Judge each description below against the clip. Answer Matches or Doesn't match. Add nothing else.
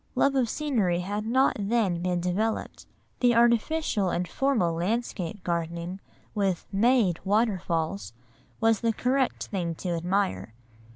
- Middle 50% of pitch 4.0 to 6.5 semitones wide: Matches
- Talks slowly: Matches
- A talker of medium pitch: Doesn't match